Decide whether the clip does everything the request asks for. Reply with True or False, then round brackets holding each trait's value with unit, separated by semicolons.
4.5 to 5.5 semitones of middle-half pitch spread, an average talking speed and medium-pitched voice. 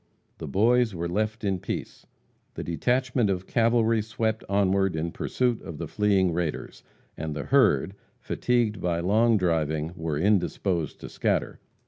False (4.9 semitones; 145 wpm; 100 Hz)